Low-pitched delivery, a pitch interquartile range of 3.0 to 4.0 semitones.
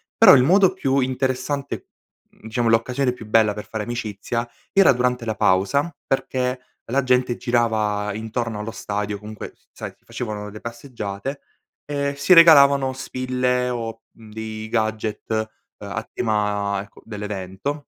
Yes: low, 115 Hz; average, 3.5 semitones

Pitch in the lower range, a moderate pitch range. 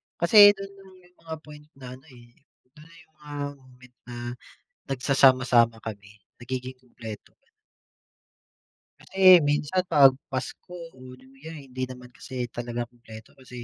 Yes: low, 130 Hz; average, 3.5 semitones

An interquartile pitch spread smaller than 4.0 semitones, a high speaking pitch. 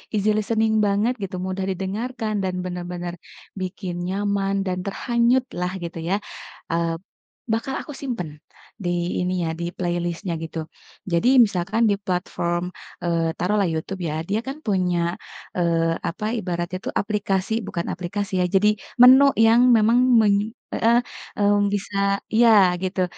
Yes: average, 3.5 semitones; high, 195 Hz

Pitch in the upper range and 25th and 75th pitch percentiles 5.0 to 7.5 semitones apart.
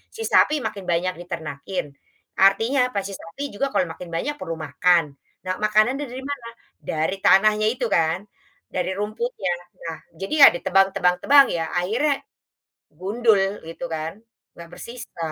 Yes: high, 195 Hz; average, 5.3 semitones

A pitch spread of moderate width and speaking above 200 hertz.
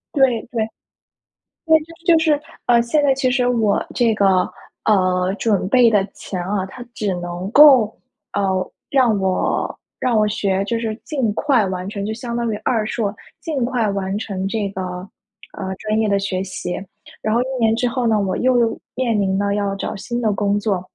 Yes: average, 3.7 semitones; high, 215 Hz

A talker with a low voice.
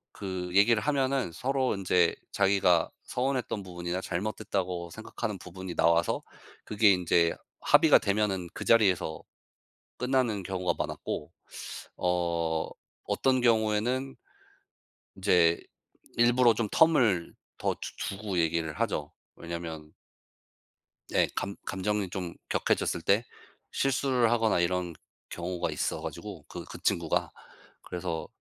Yes: very low, 95 Hz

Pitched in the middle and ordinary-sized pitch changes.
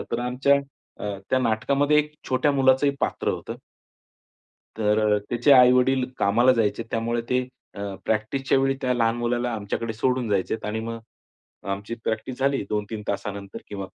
No: low, 120 Hz; average, 3.5 semitones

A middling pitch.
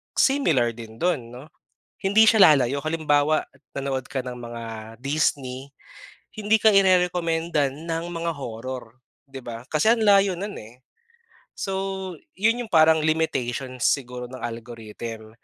Yes: medium, 145 Hz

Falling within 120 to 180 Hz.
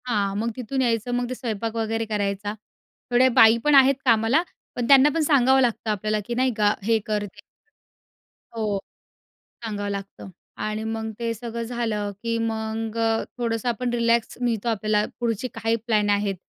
No: high, 225 Hz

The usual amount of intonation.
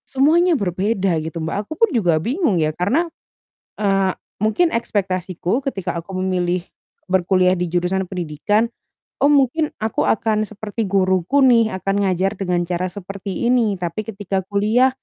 Yes: average, 3.9 semitones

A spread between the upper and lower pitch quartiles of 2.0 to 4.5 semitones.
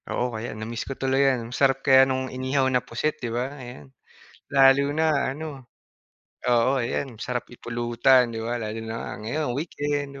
Yes: narrow, 2.5 semitones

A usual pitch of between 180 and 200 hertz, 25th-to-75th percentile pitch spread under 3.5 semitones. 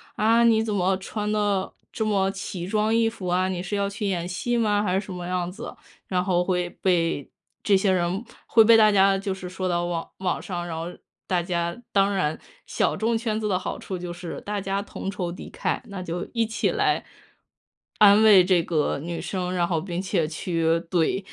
Yes: high, 190 Hz; average, 2.8 semitones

